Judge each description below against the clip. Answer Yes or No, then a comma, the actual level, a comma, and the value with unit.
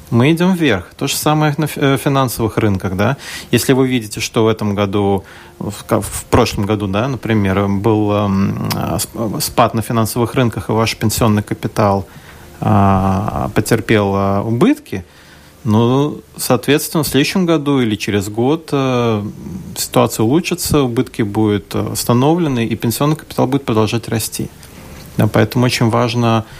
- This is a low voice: Yes, low, 115 Hz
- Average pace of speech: Yes, average, 125 wpm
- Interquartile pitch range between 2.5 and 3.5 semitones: No, average, 4.3 semitones